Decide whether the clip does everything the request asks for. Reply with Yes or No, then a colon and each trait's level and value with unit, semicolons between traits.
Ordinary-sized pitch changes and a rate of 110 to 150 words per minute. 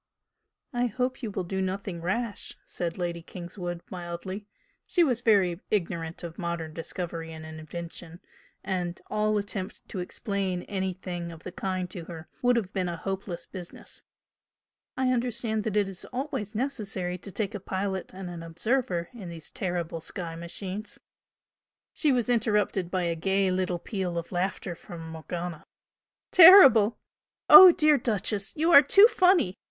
No: average, 3.9 semitones; average, 160 wpm